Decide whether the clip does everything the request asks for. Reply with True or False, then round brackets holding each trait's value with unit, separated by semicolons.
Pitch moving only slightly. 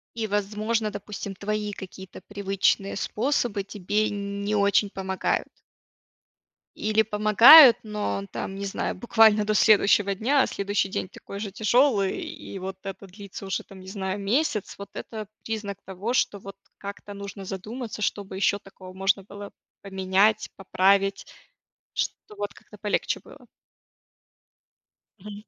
True (1.5 semitones)